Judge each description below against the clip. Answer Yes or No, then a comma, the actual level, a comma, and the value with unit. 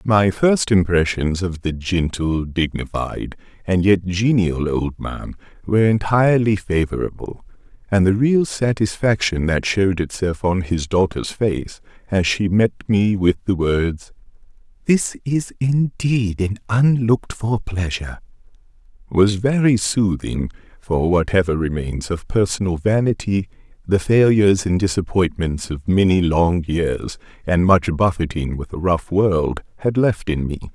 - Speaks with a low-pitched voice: Yes, very low, 95 Hz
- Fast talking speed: No, slow, 135 wpm